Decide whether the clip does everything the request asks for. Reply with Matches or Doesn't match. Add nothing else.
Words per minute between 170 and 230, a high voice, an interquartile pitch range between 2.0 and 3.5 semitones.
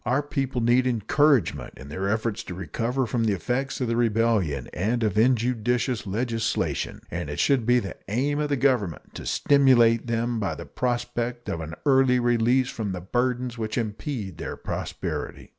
Doesn't match